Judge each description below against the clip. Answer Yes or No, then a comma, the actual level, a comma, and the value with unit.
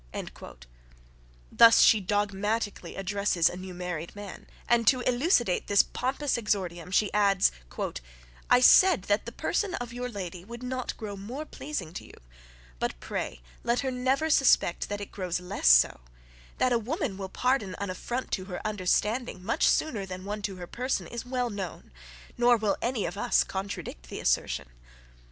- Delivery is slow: No, average, 165 wpm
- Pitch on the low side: No, high, 205 Hz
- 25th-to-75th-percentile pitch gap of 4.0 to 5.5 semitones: Yes, average, 4.8 semitones